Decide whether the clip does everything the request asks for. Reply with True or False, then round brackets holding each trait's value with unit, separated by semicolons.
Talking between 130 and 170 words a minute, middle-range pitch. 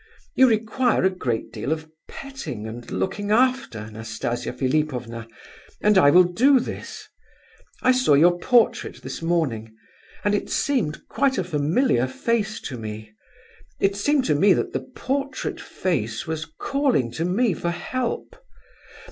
True (145 wpm; 175 Hz)